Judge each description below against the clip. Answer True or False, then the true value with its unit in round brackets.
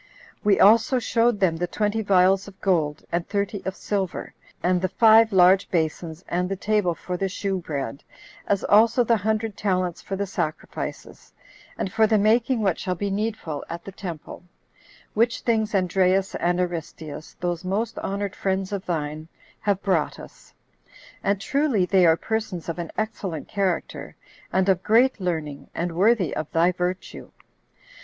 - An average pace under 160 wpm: False (165 wpm)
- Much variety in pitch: False (3.2 semitones)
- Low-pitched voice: False (190 Hz)